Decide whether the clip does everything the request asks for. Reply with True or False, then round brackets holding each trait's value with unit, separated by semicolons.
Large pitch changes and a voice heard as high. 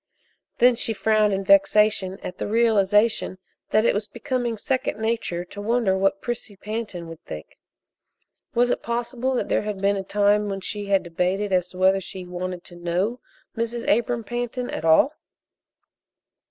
False (3.6 semitones; 205 Hz)